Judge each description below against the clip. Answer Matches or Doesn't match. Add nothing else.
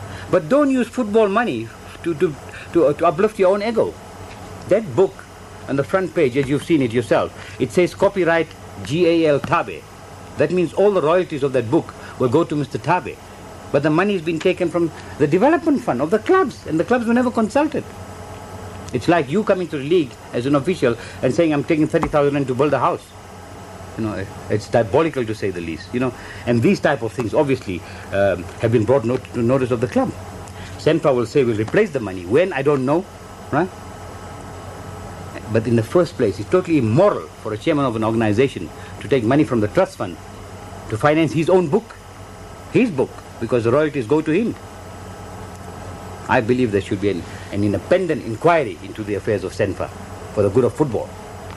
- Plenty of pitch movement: Matches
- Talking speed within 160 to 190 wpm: Doesn't match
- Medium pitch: Doesn't match